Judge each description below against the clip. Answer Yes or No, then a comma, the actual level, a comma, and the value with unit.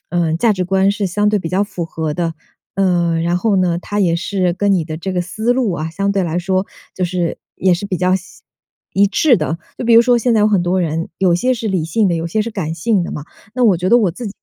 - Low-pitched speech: No, medium, 185 Hz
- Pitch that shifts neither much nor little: Yes, average, 3.3 semitones